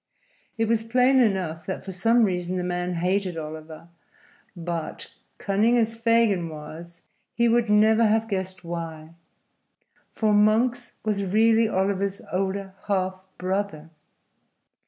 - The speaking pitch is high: Yes, high, 195 Hz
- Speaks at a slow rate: Yes, slow, 125 wpm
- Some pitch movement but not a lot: Yes, average, 4.0 semitones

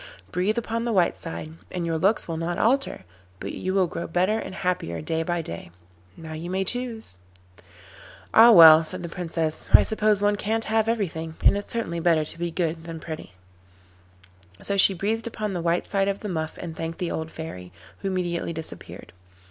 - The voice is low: No, medium, 175 Hz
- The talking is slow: No, average, 195 wpm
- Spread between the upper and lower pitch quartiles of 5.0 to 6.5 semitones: No, average, 4.1 semitones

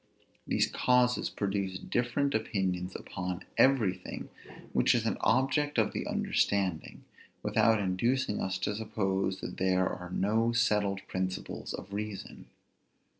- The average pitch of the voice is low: Yes, low, 100 Hz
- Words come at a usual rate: No, slow, 125 wpm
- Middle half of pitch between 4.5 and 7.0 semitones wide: No, average, 3.7 semitones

